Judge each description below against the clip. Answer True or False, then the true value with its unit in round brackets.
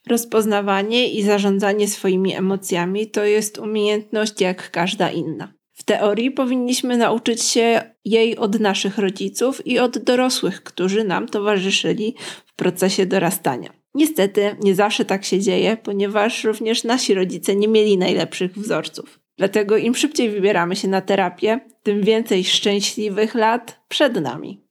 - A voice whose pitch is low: False (210 Hz)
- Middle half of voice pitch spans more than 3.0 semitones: False (2.7 semitones)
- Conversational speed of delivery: True (135 wpm)